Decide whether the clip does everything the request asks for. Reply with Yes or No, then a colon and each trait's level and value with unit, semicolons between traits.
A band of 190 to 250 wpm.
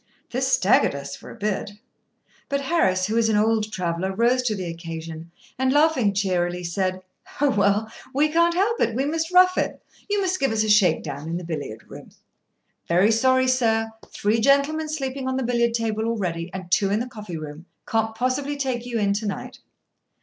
Yes: average, 195 wpm